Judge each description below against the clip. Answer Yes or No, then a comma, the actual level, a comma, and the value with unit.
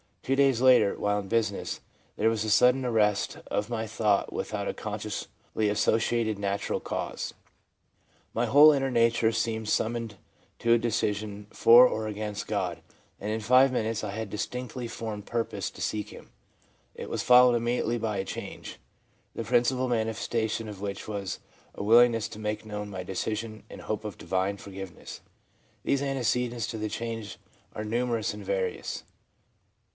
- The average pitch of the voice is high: No, low, 110 Hz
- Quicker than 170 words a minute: No, average, 160 wpm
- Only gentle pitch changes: Yes, narrow, 2.3 semitones